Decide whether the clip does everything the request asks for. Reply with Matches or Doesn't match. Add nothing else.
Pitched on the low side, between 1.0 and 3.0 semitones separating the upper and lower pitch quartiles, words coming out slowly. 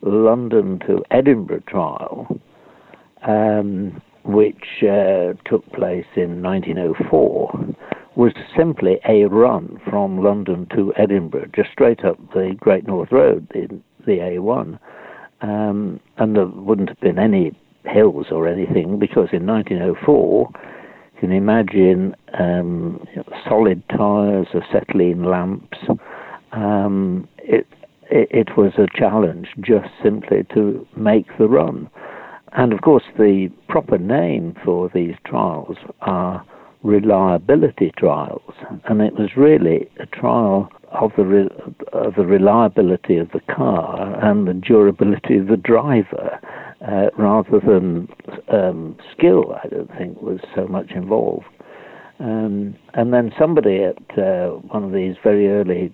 Matches